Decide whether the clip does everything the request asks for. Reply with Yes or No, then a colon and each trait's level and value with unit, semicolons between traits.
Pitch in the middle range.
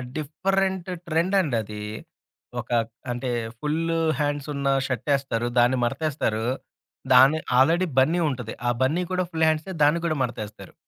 Yes: medium, 145 Hz